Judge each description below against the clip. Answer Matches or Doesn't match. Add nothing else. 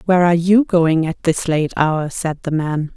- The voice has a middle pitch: Matches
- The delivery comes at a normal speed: Doesn't match